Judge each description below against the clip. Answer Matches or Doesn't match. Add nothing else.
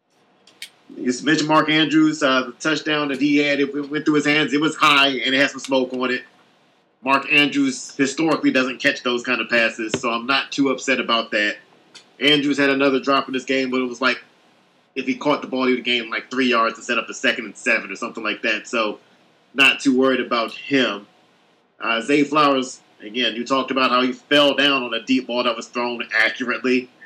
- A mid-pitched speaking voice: Doesn't match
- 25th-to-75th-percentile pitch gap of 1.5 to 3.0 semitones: Matches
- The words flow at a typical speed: Doesn't match